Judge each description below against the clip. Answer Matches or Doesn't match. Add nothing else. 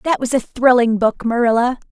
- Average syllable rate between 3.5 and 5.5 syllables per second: Matches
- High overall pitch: Matches